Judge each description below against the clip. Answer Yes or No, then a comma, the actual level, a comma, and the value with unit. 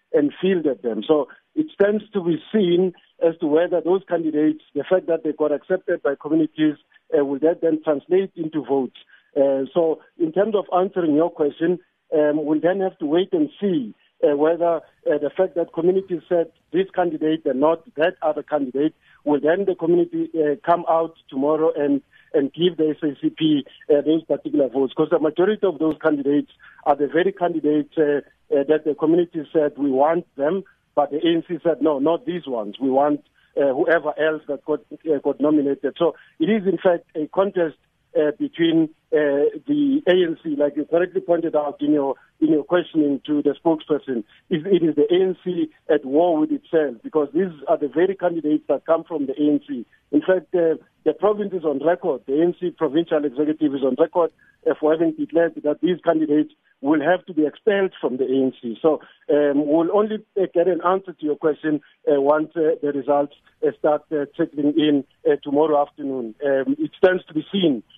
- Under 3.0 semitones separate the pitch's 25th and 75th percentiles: No, average, 3.5 semitones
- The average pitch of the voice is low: No, medium, 160 Hz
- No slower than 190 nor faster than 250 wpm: Yes, average, 195 wpm